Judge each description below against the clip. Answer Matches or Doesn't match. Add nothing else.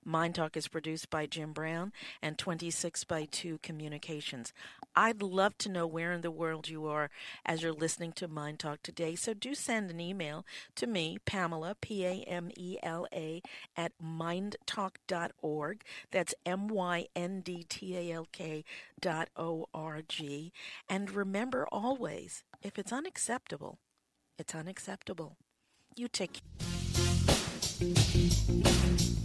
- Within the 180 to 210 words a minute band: Doesn't match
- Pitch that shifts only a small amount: Doesn't match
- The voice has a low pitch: Doesn't match